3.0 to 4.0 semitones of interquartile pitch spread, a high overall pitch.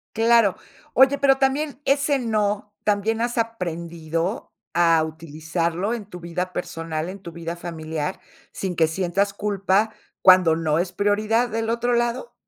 No: average, 5.3 semitones; high, 195 Hz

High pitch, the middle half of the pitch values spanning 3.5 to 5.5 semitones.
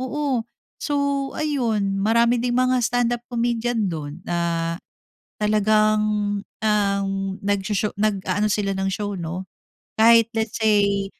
No: high, 215 Hz; average, 3.0 semitones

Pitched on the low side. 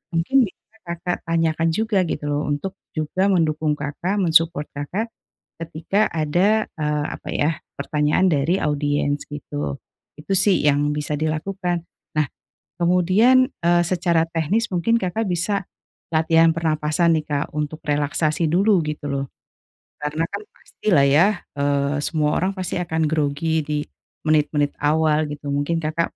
No: medium, 160 Hz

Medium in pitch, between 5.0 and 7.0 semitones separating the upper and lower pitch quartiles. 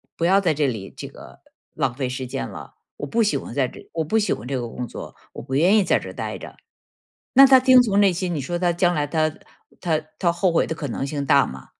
Yes: medium, 160 Hz; wide, 5.5 semitones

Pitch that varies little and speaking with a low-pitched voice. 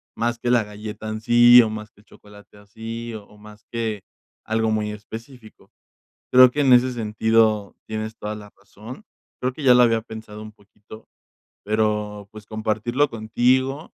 Yes: narrow, 2.0 semitones; low, 110 Hz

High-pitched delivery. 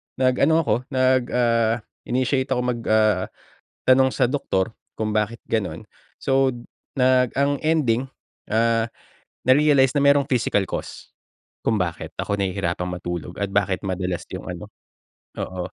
No: low, 115 Hz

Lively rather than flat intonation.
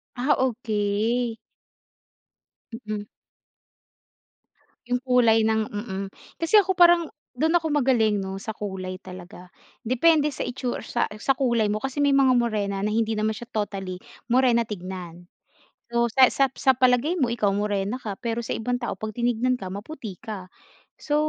No: average, 3.8 semitones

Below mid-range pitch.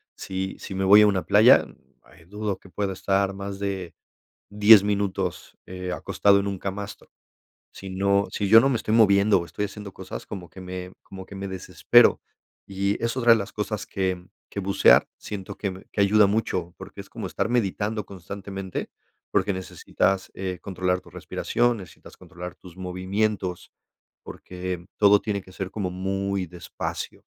Yes: very low, 95 Hz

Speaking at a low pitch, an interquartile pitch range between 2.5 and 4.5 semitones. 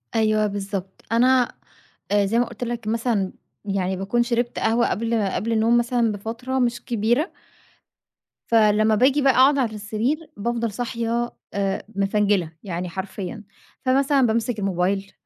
No: high, 225 Hz; average, 3.0 semitones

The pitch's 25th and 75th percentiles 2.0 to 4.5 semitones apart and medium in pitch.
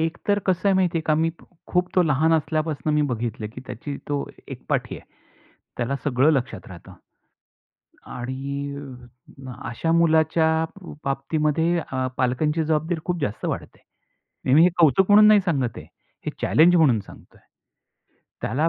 Yes: average, 3.7 semitones; medium, 155 Hz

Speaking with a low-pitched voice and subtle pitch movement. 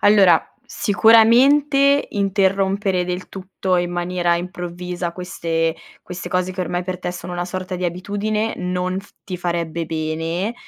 No: medium, 180 Hz; narrow, 2.1 semitones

